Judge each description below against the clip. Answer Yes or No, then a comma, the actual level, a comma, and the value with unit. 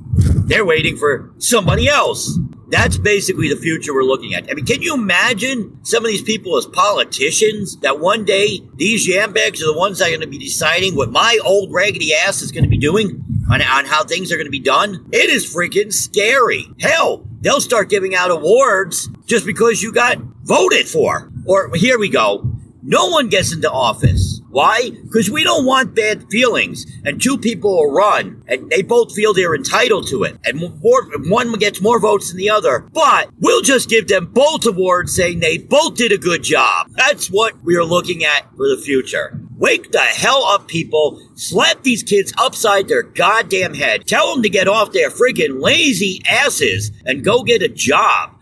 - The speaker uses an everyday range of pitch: No, wide, 7.1 semitones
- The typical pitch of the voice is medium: No, high, 205 Hz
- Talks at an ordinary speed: Yes, average, 195 wpm